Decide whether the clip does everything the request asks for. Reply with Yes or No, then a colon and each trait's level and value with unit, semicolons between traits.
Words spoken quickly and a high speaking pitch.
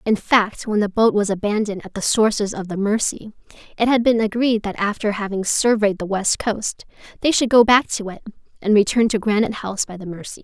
Yes: fast, 220 wpm; high, 210 Hz